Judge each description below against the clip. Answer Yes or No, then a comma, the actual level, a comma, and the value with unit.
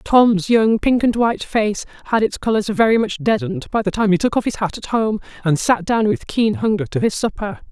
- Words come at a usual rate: No, fast, 240 wpm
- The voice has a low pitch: No, high, 220 Hz